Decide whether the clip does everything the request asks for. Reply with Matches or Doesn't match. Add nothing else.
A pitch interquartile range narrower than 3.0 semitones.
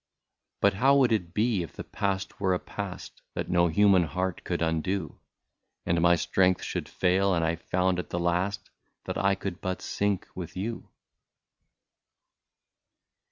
Matches